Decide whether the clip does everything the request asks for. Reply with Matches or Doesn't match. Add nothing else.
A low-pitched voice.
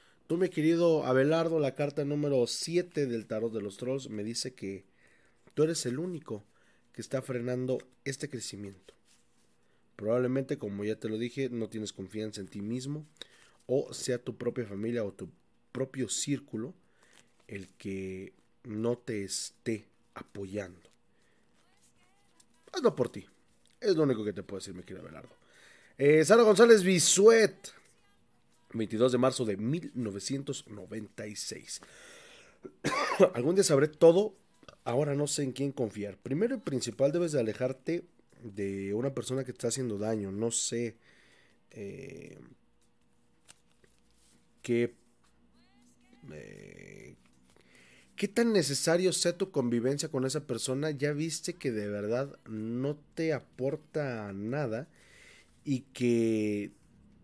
Matches